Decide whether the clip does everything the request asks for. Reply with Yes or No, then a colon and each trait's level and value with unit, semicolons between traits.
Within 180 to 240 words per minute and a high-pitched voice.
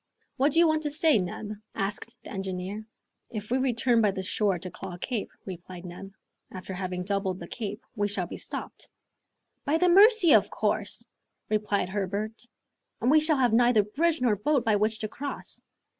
Yes: average, 190 wpm; high, 215 Hz